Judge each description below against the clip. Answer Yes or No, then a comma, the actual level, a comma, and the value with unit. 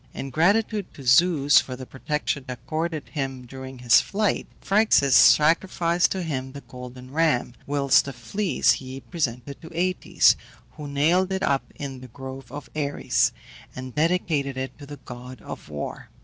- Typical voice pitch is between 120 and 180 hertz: Yes, medium, 140 Hz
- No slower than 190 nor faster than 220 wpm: No, average, 160 wpm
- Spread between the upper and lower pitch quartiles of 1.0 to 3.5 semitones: No, average, 4.3 semitones